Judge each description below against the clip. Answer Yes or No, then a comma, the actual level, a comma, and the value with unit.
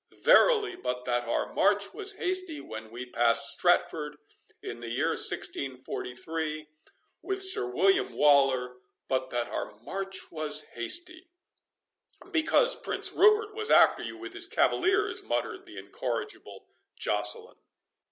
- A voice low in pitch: No, medium, 165 Hz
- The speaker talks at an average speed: No, slow, 125 wpm